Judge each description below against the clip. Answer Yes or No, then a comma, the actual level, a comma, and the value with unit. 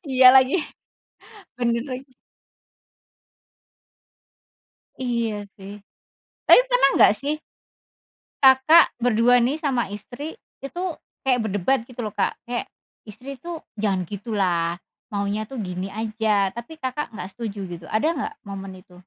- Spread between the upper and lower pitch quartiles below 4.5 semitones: No, average, 4.8 semitones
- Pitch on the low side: No, high, 235 Hz